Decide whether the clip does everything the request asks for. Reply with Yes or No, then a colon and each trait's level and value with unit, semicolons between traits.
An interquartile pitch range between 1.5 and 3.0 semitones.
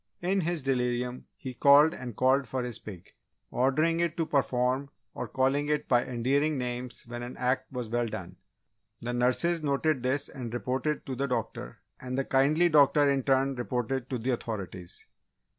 Yes: narrow, 2.6 semitones